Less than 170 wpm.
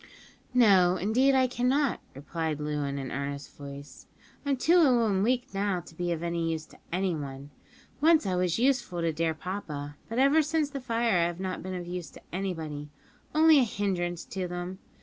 No: average, 190 wpm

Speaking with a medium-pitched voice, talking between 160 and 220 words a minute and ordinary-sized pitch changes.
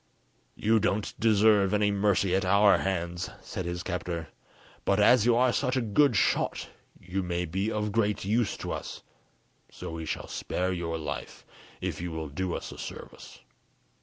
No: very low, 95 Hz; average, 170 wpm; average, 3.3 semitones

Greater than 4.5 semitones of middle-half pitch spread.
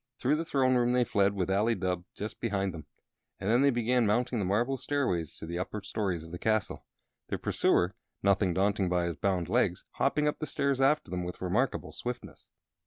Yes: average, 5.3 semitones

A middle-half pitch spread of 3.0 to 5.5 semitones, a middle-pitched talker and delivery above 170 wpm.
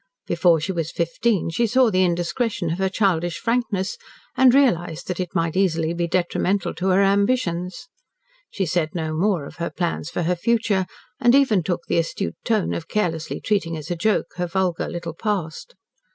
Yes: average, 3.5 semitones; medium, 180 Hz; average, 180 wpm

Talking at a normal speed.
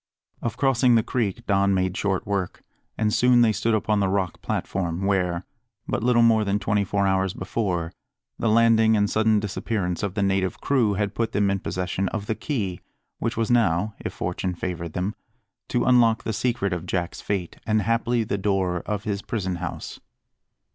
Yes: average, 185 wpm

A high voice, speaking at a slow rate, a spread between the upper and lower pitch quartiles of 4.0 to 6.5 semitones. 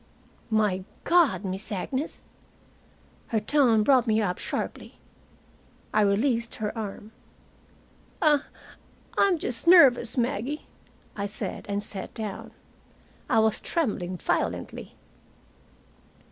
Yes: high, 220 Hz; slow, 105 wpm; average, 4.7 semitones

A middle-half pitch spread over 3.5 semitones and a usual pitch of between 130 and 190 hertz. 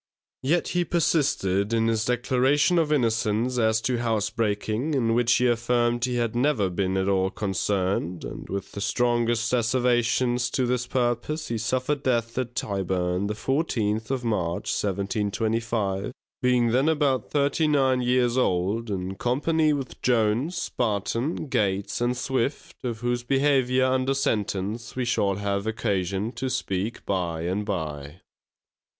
No: average, 4.0 semitones; low, 115 Hz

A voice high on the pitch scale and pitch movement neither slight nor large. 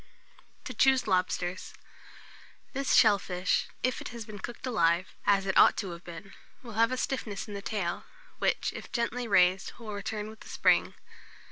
Yes: high, 205 Hz; average, 4.0 semitones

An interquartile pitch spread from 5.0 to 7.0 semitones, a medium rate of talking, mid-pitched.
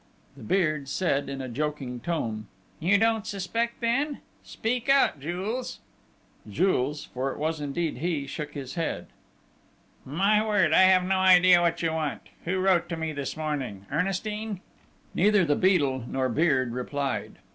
Yes: wide, 5.4 semitones; average, 155 wpm; medium, 165 Hz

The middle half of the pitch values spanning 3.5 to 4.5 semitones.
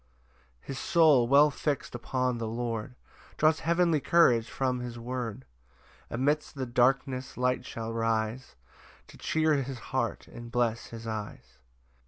No: average, 2.9 semitones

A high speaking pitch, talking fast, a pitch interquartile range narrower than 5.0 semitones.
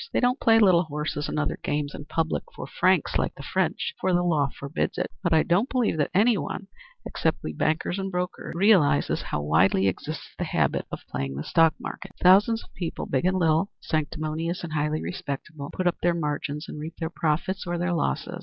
No: medium, 165 Hz; fast, 210 wpm; average, 3.6 semitones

